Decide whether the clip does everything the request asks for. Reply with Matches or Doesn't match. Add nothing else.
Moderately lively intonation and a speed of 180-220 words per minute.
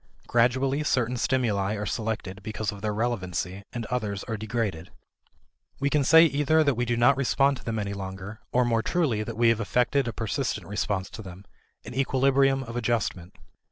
Matches